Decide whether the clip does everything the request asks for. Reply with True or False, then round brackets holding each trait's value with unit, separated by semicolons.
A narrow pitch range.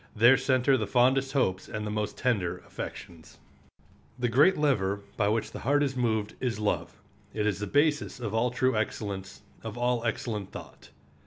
False (3.8 semitones)